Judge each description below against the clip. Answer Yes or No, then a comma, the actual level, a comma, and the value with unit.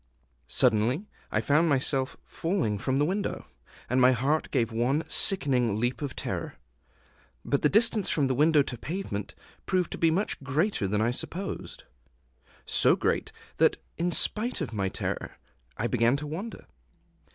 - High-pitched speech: No, medium, 140 Hz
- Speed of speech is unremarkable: Yes, average, 150 wpm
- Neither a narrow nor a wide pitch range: No, wide, 5.7 semitones